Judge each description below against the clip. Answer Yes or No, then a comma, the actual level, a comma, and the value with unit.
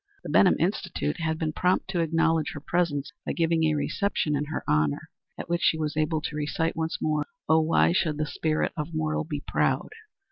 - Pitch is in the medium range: Yes, medium, 155 Hz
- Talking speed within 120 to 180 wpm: No, fast, 205 wpm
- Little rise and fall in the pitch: Yes, narrow, 1.5 semitones